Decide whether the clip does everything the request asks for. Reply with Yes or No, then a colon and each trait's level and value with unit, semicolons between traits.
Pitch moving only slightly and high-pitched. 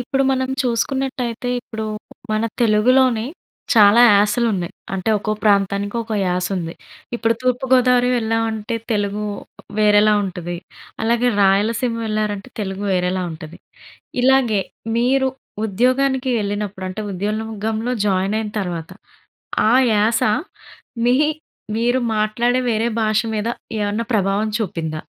No: average, 3.2 semitones; high, 215 Hz